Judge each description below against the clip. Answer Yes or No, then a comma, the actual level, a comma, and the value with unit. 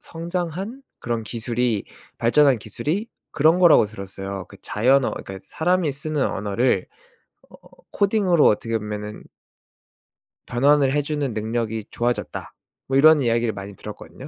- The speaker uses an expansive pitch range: Yes, wide, 6.1 semitones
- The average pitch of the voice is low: Yes, low, 125 Hz